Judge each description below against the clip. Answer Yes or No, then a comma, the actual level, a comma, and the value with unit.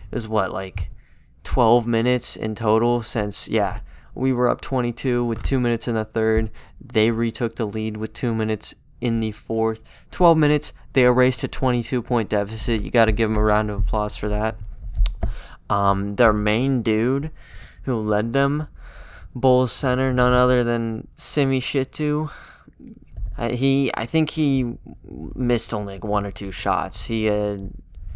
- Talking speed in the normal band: Yes, average, 165 wpm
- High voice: No, low, 115 Hz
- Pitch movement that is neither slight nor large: Yes, average, 3.1 semitones